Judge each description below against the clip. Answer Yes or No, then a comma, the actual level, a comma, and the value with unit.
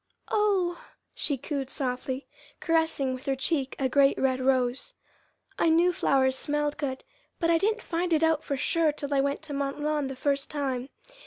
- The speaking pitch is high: Yes, very high, 285 Hz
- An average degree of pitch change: Yes, average, 3.3 semitones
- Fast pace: No, average, 180 wpm